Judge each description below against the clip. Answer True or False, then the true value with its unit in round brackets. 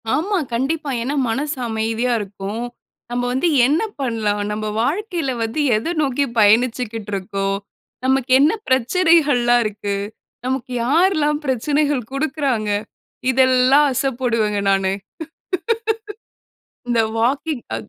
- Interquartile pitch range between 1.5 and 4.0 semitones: False (4.6 semitones)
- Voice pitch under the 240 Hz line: False (255 Hz)